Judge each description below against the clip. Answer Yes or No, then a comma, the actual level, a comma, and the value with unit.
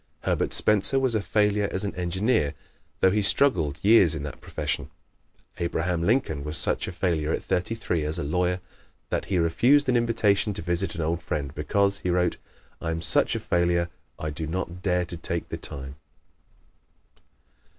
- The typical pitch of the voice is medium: No, very low, 90 Hz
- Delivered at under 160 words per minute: No, average, 180 wpm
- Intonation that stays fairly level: No, average, 3.7 semitones